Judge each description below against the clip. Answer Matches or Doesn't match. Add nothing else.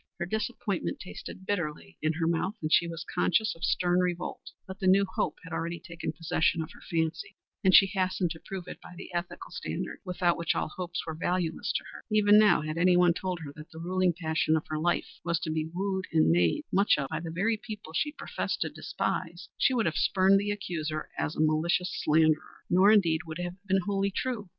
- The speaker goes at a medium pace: Doesn't match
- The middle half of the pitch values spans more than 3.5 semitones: Doesn't match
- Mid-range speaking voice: Matches